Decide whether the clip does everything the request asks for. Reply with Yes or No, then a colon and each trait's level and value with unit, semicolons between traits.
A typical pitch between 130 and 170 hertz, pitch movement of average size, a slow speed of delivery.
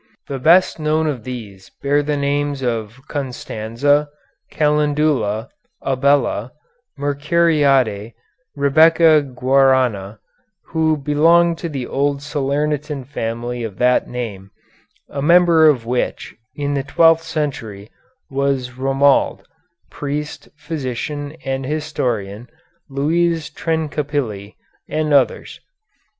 Yes: medium, 140 Hz; average, 3.3 semitones; slow, 95 wpm